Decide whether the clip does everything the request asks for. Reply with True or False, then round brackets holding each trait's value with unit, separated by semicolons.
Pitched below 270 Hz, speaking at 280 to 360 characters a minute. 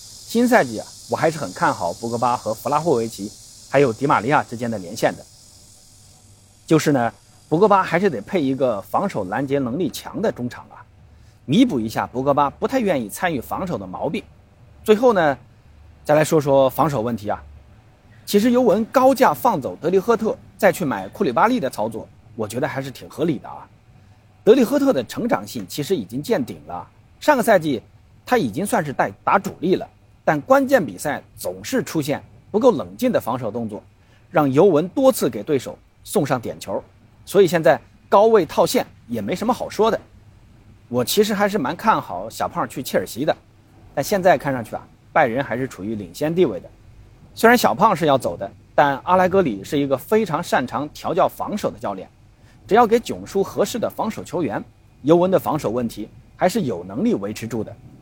True (135 Hz; 285 characters per minute)